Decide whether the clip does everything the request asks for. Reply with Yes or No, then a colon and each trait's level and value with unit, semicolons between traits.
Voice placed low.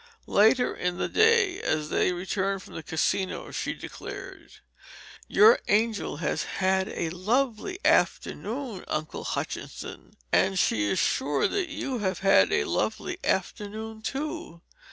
No: high, 210 Hz